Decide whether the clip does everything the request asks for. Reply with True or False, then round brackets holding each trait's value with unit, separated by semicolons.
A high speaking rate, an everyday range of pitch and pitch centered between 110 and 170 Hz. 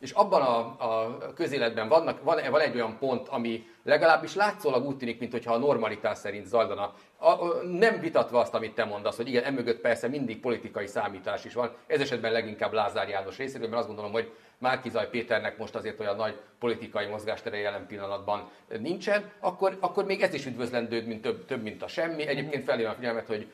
False (190 wpm; 5.7 semitones; 120 Hz)